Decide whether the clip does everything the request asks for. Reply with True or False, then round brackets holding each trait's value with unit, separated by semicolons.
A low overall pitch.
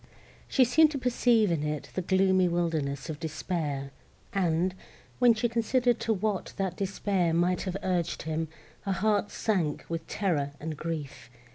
False (180 Hz)